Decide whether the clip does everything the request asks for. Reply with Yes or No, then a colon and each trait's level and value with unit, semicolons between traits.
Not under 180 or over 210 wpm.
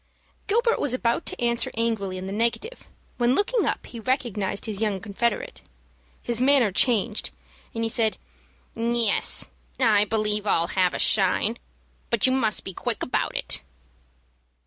No: average, 150 wpm